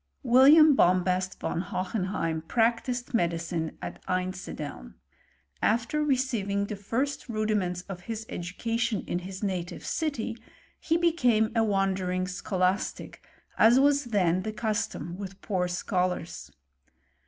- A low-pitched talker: No, high, 200 Hz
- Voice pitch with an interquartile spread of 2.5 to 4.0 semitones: No, average, 4.4 semitones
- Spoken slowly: Yes, slow, 120 wpm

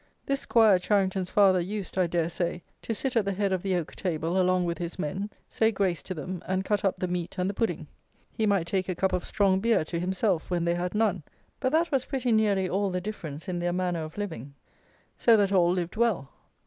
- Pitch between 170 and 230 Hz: Yes, medium, 185 Hz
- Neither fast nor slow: No, fast, 235 wpm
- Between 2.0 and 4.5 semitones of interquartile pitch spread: Yes, average, 2.8 semitones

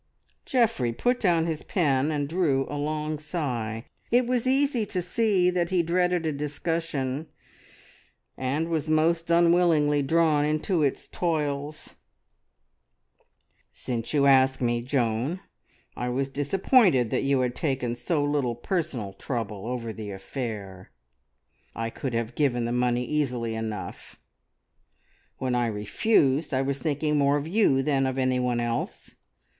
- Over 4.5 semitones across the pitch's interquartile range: Yes, average, 5.1 semitones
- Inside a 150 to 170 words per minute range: No, average, 140 wpm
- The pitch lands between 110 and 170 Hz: Yes, medium, 140 Hz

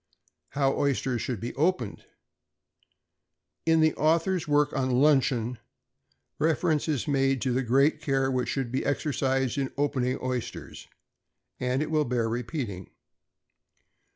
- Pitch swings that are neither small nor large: Yes, average, 3.0 semitones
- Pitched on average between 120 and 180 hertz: Yes, low, 135 Hz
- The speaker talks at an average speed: No, slow, 125 wpm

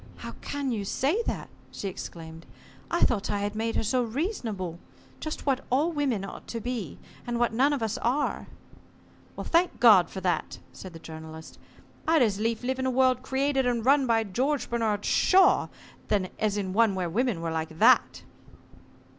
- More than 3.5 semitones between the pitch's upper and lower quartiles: Yes, average, 5.1 semitones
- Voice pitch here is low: No, high, 230 Hz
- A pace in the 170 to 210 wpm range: Yes, average, 180 wpm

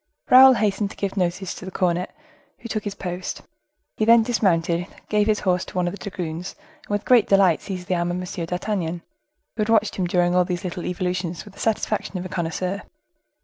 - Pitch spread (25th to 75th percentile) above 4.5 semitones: No, average, 2.7 semitones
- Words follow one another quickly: Yes, fast, 215 wpm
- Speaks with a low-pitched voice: No, medium, 185 Hz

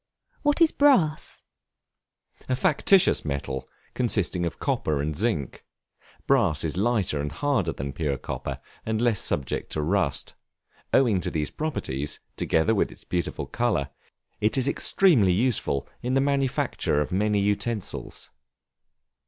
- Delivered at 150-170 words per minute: No, slow, 135 wpm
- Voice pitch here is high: No, low, 100 Hz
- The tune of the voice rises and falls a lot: Yes, wide, 9.0 semitones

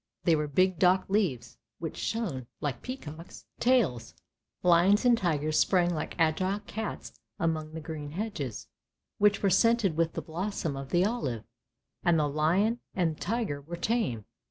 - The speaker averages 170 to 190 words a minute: No, average, 155 wpm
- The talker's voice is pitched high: No, medium, 170 Hz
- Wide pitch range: No, average, 5.0 semitones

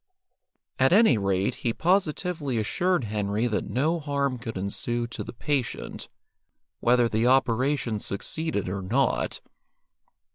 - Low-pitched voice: Yes, low, 125 Hz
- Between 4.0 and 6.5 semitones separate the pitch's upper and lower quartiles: Yes, average, 5.0 semitones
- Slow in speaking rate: Yes, slow, 120 wpm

